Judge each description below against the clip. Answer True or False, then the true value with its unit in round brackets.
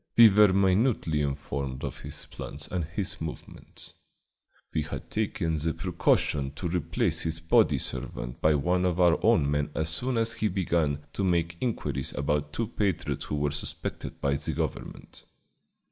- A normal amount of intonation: True (4.4 semitones)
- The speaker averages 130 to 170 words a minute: True (160 wpm)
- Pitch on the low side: True (80 Hz)